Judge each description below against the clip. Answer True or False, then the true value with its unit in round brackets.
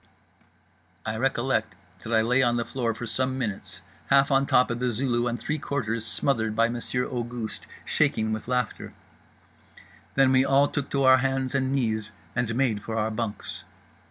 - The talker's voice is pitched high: False (120 Hz)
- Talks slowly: False (175 wpm)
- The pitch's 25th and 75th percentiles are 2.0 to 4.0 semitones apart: True (2.9 semitones)